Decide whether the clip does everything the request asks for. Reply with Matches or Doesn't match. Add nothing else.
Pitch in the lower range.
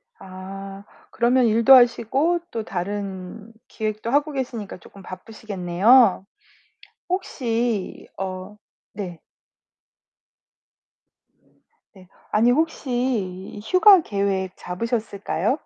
Doesn't match